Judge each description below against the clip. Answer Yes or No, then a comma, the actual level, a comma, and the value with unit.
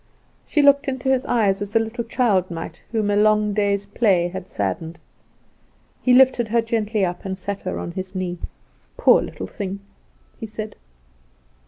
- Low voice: No, high, 205 Hz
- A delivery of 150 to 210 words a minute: Yes, average, 170 wpm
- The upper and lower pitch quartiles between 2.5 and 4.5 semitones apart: Yes, average, 3.5 semitones